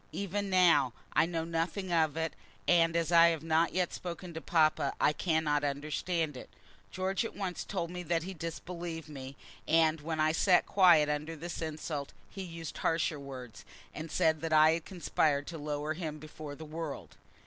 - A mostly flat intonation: Yes, narrow, 2.1 semitones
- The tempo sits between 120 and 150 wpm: No, average, 180 wpm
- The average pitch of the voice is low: No, medium, 160 Hz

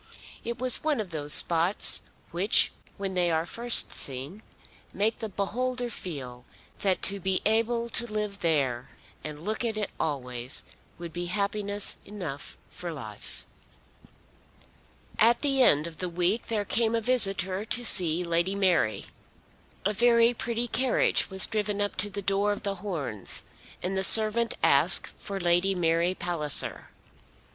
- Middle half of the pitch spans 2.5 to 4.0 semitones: No, average, 4.4 semitones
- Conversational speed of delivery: Yes, average, 150 wpm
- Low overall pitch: No, high, 195 Hz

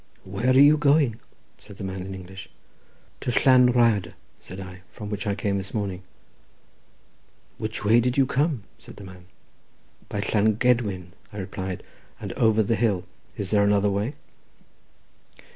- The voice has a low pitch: Yes, low, 105 Hz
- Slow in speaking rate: No, average, 160 wpm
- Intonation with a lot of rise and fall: No, average, 3.8 semitones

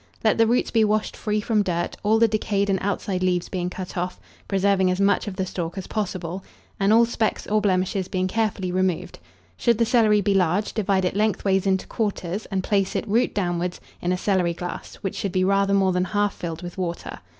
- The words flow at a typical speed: No, fast, 215 wpm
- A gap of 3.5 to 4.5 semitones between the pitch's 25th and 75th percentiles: No, narrow, 2.4 semitones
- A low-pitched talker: No, high, 195 Hz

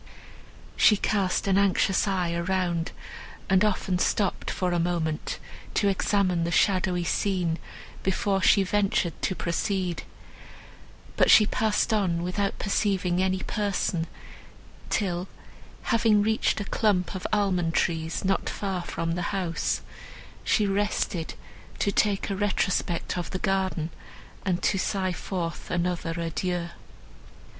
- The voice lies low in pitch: No, medium, 185 Hz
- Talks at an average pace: No, slow, 125 wpm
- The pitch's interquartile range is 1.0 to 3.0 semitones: Yes, narrow, 2.4 semitones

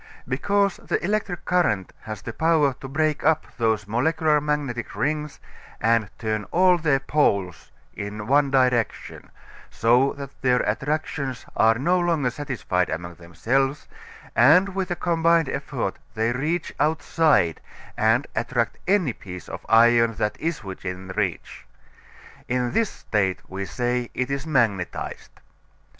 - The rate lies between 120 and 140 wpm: Yes, slow, 135 wpm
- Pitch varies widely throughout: Yes, wide, 5.8 semitones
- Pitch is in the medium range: No, low, 130 Hz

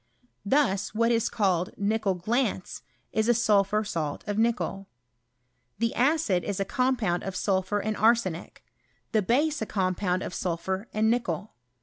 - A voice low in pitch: No, high, 210 Hz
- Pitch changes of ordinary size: Yes, average, 3.5 semitones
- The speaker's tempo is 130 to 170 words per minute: Yes, average, 145 wpm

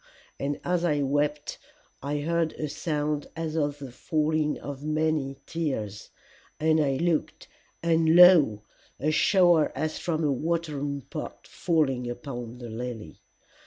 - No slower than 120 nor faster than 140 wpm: Yes, slow, 135 wpm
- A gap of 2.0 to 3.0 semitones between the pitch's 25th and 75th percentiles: Yes, average, 2.7 semitones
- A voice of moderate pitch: Yes, medium, 150 Hz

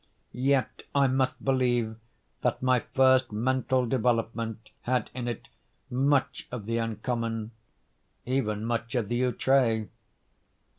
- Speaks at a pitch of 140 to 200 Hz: No, low, 120 Hz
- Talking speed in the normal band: No, slow, 110 wpm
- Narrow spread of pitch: Yes, narrow, 2.3 semitones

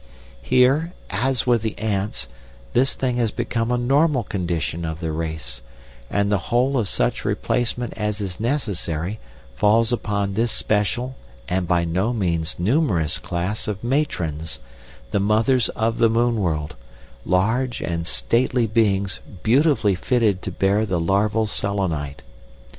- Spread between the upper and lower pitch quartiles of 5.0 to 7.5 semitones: Yes, average, 5.3 semitones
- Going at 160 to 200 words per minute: No, average, 140 wpm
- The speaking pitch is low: Yes, low, 105 Hz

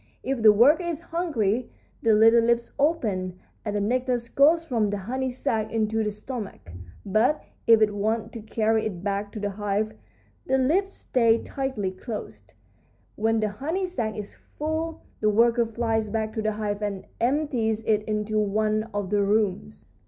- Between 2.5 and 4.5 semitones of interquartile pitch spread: Yes, average, 3.3 semitones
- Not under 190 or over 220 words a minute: No, average, 170 wpm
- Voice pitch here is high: Yes, high, 220 Hz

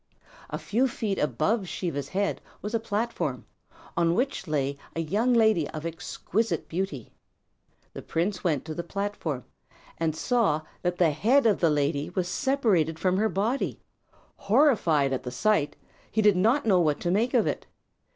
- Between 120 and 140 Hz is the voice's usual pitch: No, medium, 185 Hz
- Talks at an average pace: Yes, average, 165 wpm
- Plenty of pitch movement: Yes, wide, 5.7 semitones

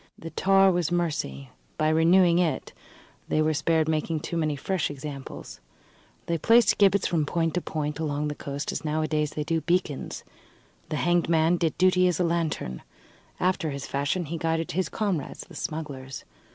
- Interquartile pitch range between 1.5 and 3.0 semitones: Yes, average, 2.7 semitones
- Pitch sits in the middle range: Yes, medium, 160 Hz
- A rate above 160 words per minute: Yes, average, 170 wpm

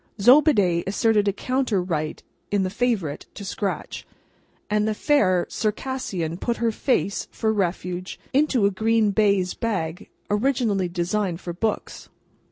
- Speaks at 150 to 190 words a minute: No, slow, 135 wpm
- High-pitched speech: Yes, high, 205 Hz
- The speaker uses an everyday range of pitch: Yes, average, 3.9 semitones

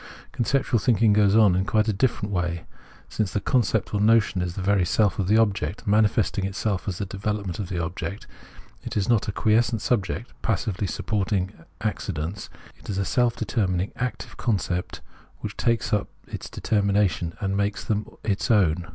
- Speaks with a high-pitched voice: No, low, 100 Hz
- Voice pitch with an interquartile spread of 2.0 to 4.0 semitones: Yes, narrow, 2.5 semitones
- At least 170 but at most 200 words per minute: Yes, average, 175 wpm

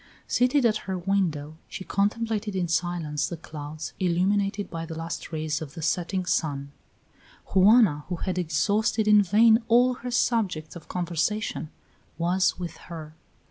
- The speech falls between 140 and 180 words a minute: Yes, average, 145 wpm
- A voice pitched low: No, medium, 180 Hz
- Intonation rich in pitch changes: No, average, 4.4 semitones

